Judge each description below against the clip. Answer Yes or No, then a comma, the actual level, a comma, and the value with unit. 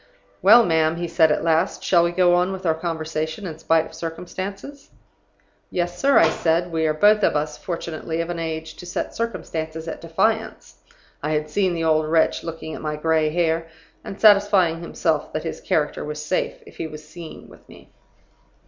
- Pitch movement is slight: Yes, narrow, 2.1 semitones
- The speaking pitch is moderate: Yes, medium, 165 Hz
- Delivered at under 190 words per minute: No, average, 195 wpm